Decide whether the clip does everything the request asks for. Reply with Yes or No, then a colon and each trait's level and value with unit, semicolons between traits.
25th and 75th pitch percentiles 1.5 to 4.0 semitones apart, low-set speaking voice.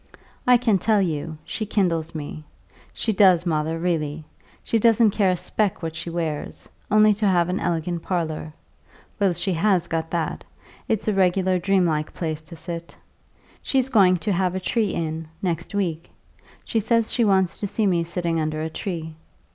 No: average, 3.7 semitones; medium, 175 Hz